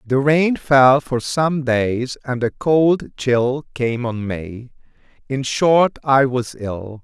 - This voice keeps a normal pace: Yes, average, 155 wpm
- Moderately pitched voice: No, low, 130 Hz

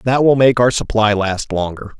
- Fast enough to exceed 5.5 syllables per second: No, 4.9 syllables/s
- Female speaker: No, male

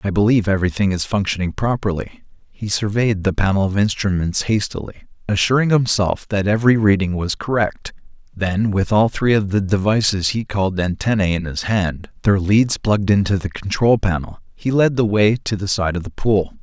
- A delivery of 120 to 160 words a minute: No, average, 180 wpm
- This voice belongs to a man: Yes, male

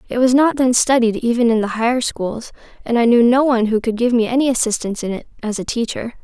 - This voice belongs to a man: No, female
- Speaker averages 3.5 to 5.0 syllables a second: No, 6.3 syllables/s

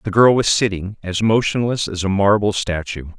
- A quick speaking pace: No, average, 190 wpm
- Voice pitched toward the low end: Yes, low, 100 Hz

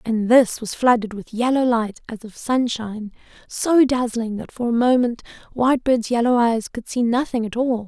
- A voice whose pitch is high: Yes, high, 235 Hz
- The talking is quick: No, average, 185 wpm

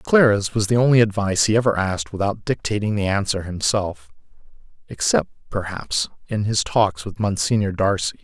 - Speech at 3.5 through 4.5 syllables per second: No, 5.3 syllables/s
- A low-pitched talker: Yes, low, 100 Hz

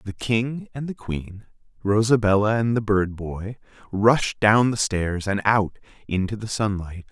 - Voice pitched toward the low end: Yes, low, 105 Hz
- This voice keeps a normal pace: Yes, average, 160 wpm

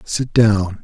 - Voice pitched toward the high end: No, low, 105 Hz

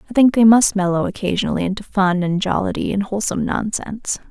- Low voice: No, high, 205 Hz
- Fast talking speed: No, average, 180 wpm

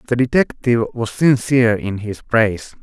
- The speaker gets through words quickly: No, average, 150 wpm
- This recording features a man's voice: Yes, male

